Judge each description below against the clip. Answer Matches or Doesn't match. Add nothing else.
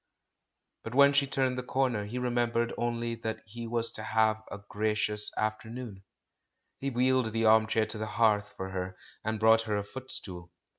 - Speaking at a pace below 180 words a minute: Doesn't match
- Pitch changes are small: Matches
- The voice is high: Doesn't match